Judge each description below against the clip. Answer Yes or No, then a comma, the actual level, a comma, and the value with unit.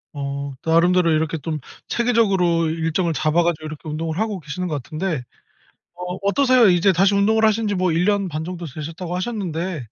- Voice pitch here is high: No, medium, 175 Hz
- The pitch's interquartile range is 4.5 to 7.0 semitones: No, average, 3.8 semitones